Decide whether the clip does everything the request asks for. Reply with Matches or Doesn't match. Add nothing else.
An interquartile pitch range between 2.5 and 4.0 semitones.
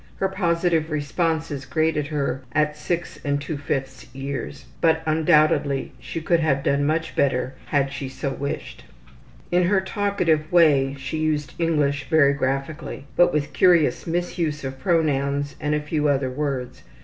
Matches